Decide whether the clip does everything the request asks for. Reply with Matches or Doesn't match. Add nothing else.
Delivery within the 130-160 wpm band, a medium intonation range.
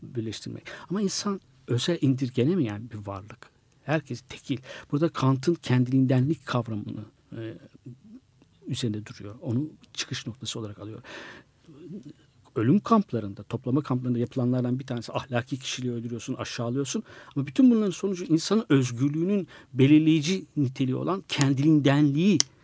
Doesn't match